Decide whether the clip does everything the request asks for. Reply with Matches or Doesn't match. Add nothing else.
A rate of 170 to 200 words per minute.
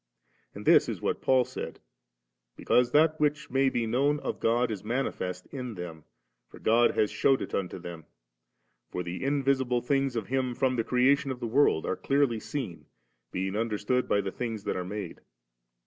Matches